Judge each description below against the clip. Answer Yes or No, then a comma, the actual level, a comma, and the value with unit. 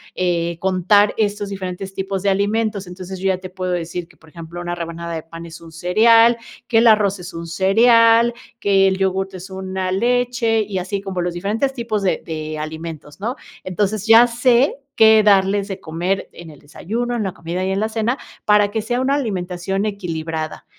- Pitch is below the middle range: No, high, 190 Hz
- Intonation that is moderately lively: Yes, average, 3.8 semitones